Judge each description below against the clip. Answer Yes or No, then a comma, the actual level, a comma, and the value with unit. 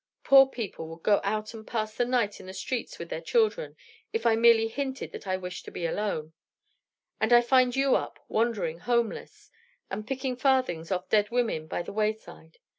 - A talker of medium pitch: No, high, 225 Hz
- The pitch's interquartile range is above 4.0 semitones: Yes, average, 4.6 semitones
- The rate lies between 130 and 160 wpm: No, average, 190 wpm